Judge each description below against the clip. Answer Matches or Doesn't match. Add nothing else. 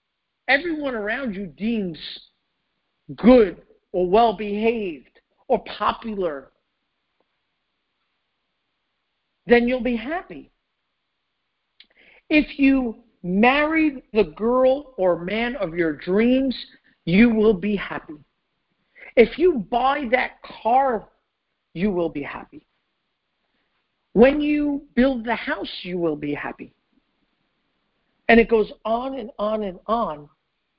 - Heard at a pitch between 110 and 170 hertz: Doesn't match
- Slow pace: Matches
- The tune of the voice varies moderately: Matches